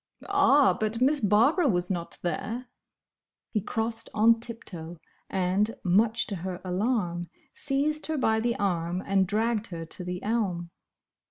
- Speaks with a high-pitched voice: Yes, high, 210 Hz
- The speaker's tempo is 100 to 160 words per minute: Yes, average, 150 wpm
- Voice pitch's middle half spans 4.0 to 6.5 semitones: Yes, average, 4.6 semitones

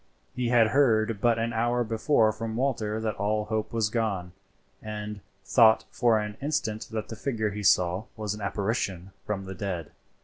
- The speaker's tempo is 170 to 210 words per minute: Yes, average, 175 wpm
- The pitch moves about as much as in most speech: No, narrow, 1.6 semitones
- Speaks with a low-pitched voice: Yes, low, 110 Hz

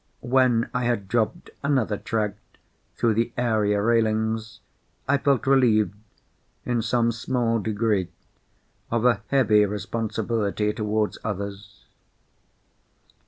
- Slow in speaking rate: Yes, slow, 105 wpm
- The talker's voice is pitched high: No, low, 110 Hz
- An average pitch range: No, narrow, 2.2 semitones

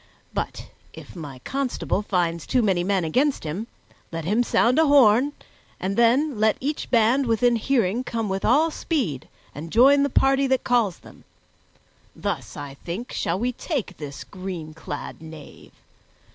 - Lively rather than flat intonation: Yes, wide, 6.9 semitones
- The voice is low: No, high, 225 Hz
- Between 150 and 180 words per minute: Yes, average, 160 wpm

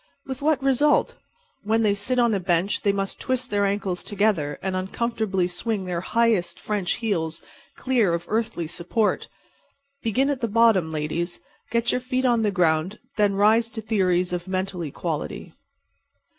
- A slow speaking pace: No, average, 165 wpm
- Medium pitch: No, high, 205 Hz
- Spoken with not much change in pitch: No, average, 4.4 semitones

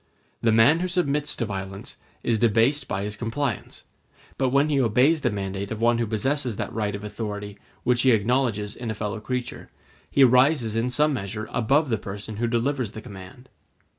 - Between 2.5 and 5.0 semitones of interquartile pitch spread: Yes, average, 4.0 semitones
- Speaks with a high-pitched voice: No, low, 115 Hz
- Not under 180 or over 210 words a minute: Yes, average, 190 wpm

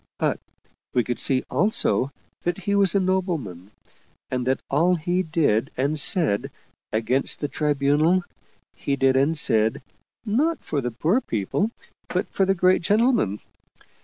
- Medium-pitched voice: Yes, medium, 155 Hz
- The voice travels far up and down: Yes, wide, 6.3 semitones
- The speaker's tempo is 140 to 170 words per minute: Yes, average, 150 wpm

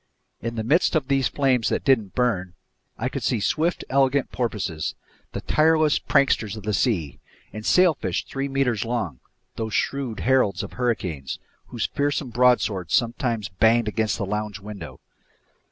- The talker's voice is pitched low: Yes, low, 115 Hz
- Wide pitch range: No, average, 4.5 semitones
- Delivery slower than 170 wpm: Yes, average, 155 wpm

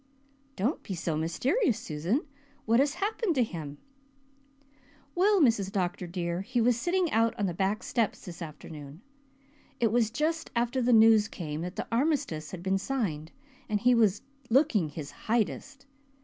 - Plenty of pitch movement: Yes, wide, 6.7 semitones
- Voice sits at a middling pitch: No, high, 220 Hz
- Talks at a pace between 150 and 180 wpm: Yes, average, 160 wpm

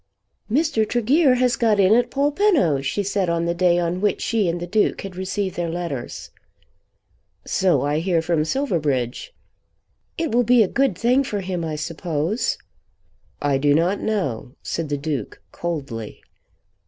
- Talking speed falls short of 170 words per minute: Yes, average, 160 wpm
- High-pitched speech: No, medium, 180 Hz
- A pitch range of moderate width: No, wide, 6.1 semitones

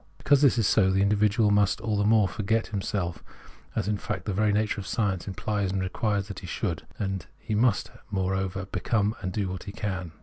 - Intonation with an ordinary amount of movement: No, narrow, 1.9 semitones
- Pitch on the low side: Yes, low, 100 Hz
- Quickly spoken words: Yes, fast, 215 wpm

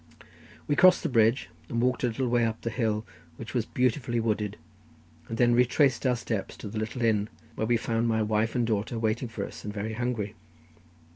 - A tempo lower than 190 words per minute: No, average, 200 wpm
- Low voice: Yes, low, 115 Hz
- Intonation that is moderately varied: No, narrow, 2.0 semitones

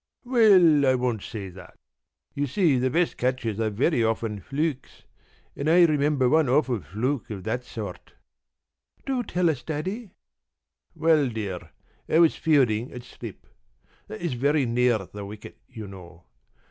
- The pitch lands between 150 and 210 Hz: No, low, 125 Hz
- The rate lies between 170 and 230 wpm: No, average, 155 wpm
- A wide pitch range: Yes, wide, 6.1 semitones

